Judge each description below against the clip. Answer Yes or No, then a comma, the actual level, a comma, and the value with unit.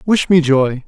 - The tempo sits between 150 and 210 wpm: Yes, fast, 205 wpm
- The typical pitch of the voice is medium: Yes, medium, 155 Hz